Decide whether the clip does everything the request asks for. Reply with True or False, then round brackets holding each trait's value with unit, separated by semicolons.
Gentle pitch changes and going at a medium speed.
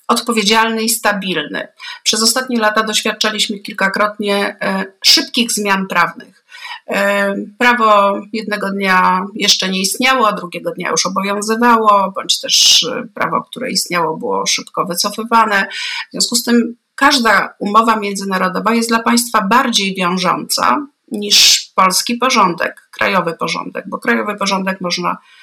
False (3.4 semitones; 120 wpm)